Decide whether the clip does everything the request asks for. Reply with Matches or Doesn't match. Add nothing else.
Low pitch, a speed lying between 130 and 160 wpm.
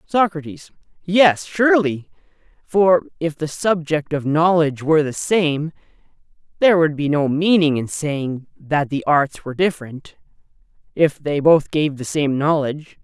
Doesn't match